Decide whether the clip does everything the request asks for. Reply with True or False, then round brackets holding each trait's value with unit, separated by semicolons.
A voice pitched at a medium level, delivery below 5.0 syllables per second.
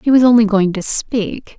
False (220 Hz; 4.7 syllables/s)